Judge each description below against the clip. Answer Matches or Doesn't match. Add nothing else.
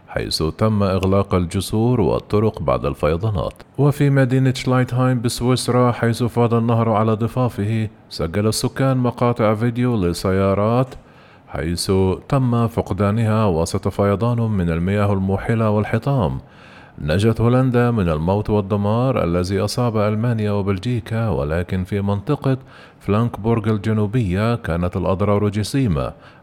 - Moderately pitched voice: Doesn't match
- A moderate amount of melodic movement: Matches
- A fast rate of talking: Doesn't match